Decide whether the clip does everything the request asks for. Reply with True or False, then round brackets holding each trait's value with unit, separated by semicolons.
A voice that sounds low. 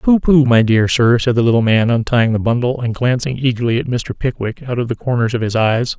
True (120 Hz)